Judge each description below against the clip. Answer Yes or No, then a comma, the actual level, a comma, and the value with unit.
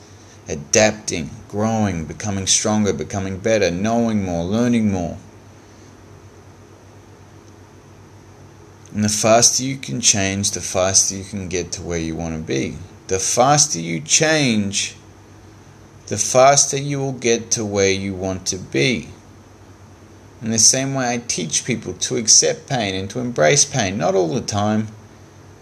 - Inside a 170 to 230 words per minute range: No, average, 140 wpm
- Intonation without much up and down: Yes, narrow, 2.3 semitones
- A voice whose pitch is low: Yes, low, 105 Hz